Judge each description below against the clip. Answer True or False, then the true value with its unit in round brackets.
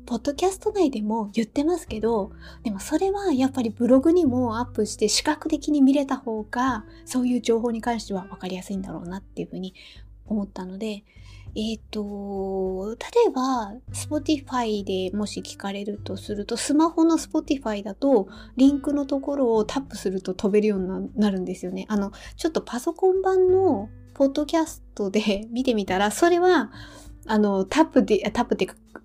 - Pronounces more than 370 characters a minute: True (380 characters per minute)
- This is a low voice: False (225 Hz)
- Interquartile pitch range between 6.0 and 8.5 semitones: True (6.3 semitones)